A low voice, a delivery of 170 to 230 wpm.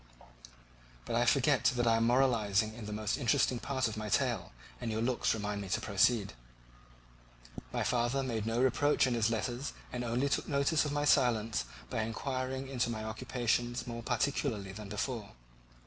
Yes: low, 120 Hz; average, 175 wpm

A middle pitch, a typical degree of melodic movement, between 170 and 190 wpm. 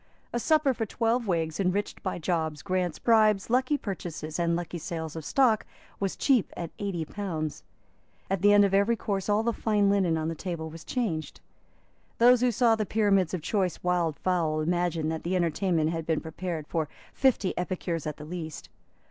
Yes: medium, 180 Hz; average, 4.4 semitones; average, 185 wpm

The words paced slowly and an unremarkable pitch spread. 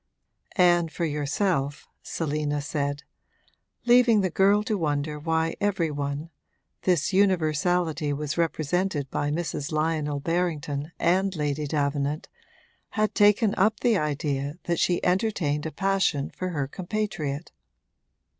Yes: slow, 120 wpm; average, 4.2 semitones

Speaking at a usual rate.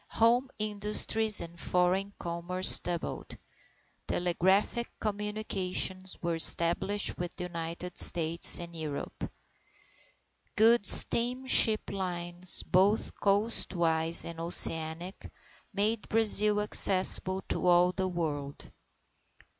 No: slow, 90 wpm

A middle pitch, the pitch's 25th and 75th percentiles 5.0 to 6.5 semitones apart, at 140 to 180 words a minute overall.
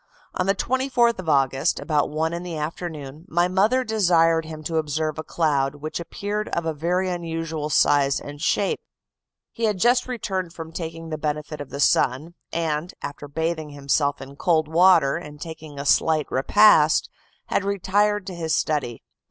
No: medium, 160 Hz; average, 3.6 semitones; average, 170 wpm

